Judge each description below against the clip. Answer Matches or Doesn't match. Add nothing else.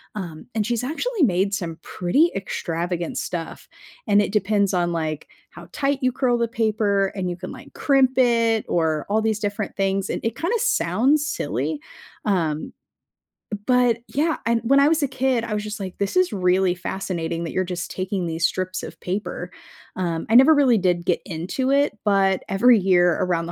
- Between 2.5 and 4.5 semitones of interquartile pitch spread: Doesn't match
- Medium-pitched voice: Doesn't match